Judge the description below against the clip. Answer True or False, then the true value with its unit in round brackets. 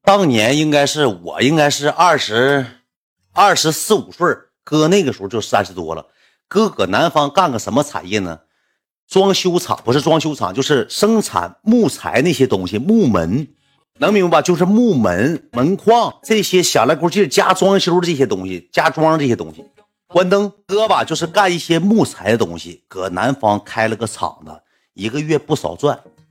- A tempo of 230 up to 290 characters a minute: True (270 characters per minute)